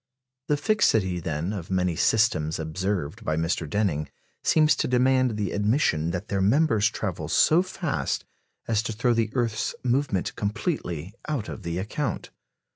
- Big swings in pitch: Yes, wide, 6.1 semitones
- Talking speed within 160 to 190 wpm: No, average, 150 wpm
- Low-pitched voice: Yes, low, 105 Hz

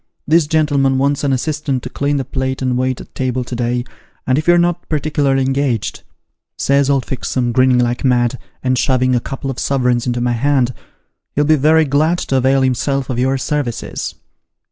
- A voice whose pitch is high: No, low, 135 Hz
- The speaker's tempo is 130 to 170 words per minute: No, average, 195 wpm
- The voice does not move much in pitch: Yes, narrow, 2.3 semitones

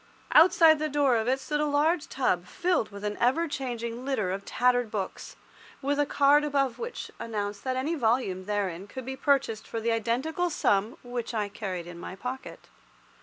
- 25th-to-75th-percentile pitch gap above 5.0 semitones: Yes, wide, 5.5 semitones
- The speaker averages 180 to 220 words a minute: Yes, average, 185 wpm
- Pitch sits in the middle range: No, high, 245 Hz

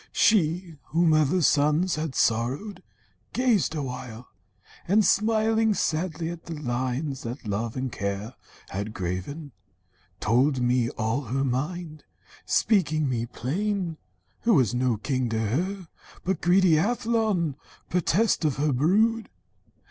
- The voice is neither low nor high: Yes, medium, 150 Hz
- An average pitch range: No, wide, 6.8 semitones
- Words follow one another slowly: Yes, slow, 125 wpm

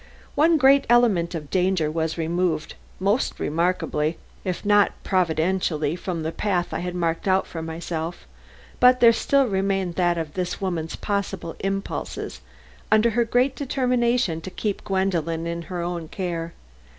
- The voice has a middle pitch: Yes, medium, 180 Hz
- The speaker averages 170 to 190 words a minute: No, average, 150 wpm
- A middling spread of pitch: Yes, average, 3.8 semitones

